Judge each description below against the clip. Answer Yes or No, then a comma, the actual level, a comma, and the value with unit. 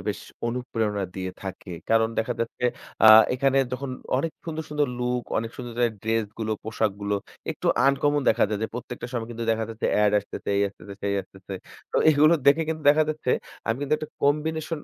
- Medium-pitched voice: No, low, 120 Hz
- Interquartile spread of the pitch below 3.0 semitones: No, average, 4.7 semitones